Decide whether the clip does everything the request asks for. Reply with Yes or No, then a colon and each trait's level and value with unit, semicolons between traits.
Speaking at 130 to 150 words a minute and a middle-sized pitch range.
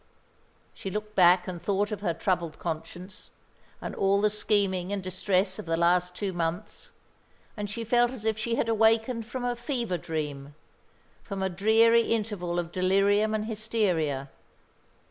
No: average, 160 wpm; average, 3.7 semitones